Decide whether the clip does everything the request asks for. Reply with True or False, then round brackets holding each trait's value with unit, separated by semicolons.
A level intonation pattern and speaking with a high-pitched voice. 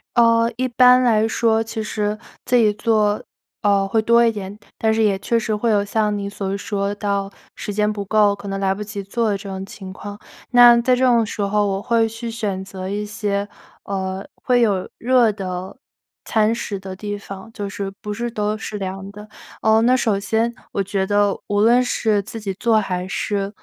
True (2.3 semitones; 210 Hz)